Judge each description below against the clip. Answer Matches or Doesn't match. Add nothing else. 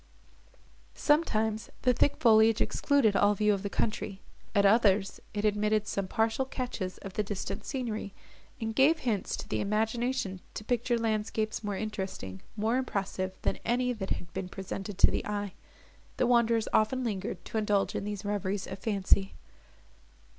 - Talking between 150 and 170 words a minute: Matches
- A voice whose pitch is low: Doesn't match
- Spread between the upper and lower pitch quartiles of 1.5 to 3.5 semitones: Matches